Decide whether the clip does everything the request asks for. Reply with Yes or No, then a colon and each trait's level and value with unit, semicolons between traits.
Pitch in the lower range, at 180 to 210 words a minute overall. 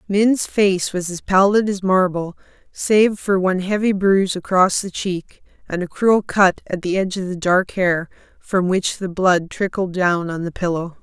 No: medium, 185 Hz; average, 190 wpm